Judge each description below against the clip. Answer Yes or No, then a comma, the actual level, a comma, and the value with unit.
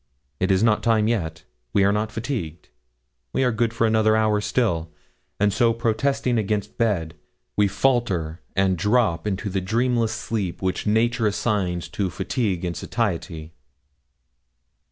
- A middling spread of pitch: Yes, average, 3.7 semitones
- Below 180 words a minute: Yes, average, 145 wpm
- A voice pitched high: No, low, 105 Hz